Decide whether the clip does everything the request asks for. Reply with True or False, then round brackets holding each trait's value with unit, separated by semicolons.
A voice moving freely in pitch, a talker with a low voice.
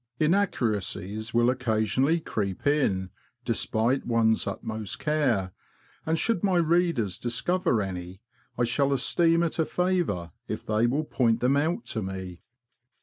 True (6.7 semitones; 120 Hz)